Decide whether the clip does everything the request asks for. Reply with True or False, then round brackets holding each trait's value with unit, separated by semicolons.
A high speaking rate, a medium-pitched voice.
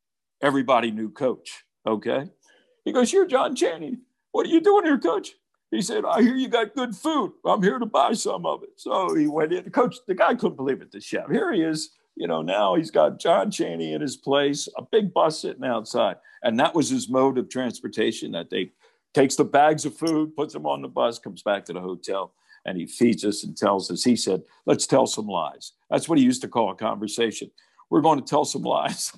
True (230 wpm; 160 Hz)